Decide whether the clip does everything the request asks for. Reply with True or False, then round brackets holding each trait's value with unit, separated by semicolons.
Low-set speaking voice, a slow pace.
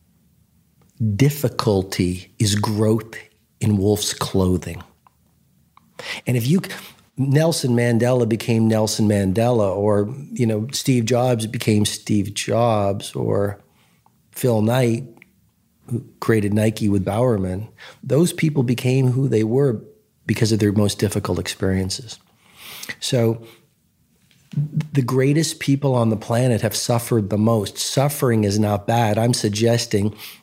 True (115 Hz; 115 wpm)